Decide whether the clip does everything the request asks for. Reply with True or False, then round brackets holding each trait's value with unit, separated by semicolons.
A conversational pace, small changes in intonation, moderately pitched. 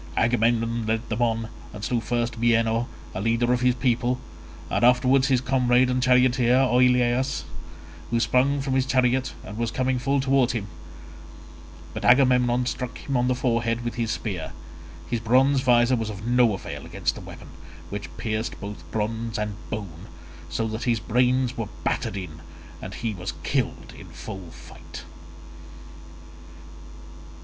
False (155 wpm; 2.1 semitones; 120 Hz)